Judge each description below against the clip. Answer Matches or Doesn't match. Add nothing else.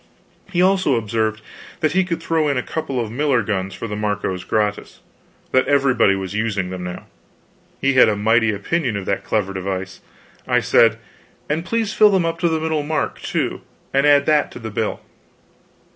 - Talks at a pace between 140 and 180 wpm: Doesn't match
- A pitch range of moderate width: Doesn't match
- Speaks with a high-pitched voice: Doesn't match